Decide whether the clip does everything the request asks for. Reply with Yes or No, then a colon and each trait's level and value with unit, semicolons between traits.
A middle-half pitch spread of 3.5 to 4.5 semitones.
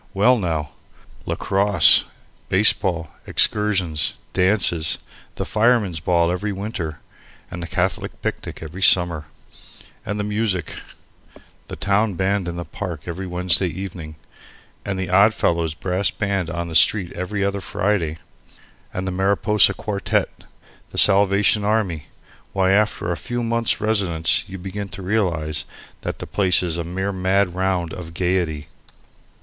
No: average, 2.8 semitones